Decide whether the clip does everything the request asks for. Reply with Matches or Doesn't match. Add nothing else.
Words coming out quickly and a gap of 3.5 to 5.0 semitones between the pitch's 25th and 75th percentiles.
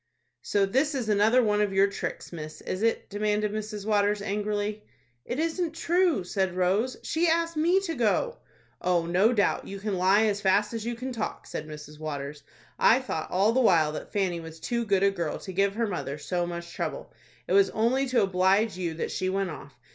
Matches